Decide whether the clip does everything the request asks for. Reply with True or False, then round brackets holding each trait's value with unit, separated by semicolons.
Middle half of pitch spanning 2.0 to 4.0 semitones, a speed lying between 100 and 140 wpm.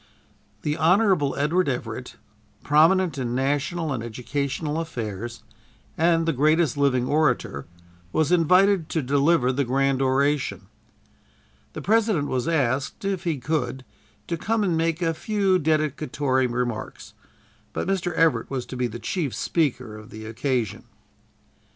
False (4.6 semitones; 135 wpm)